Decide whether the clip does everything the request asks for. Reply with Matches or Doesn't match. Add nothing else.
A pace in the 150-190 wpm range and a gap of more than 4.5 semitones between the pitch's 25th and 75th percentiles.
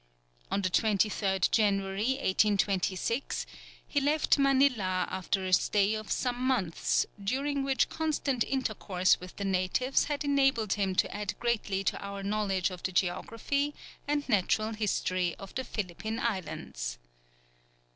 Doesn't match